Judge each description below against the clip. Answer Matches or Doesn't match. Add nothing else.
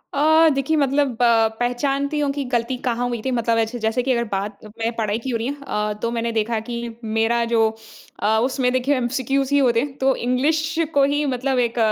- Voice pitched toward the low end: Doesn't match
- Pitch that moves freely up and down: Doesn't match